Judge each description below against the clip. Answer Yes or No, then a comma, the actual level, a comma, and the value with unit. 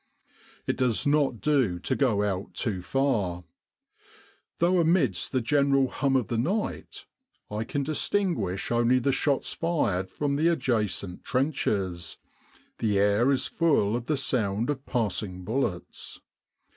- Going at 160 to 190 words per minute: No, slow, 135 wpm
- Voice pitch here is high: No, low, 125 Hz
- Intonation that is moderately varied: No, wide, 5.8 semitones